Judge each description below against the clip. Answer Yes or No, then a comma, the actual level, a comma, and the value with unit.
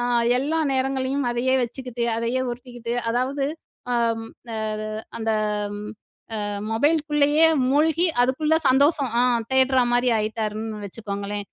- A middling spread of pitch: Yes, average, 3.5 semitones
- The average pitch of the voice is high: Yes, very high, 250 Hz